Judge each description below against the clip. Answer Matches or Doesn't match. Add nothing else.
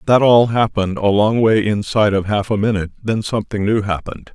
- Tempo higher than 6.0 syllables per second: Matches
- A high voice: Doesn't match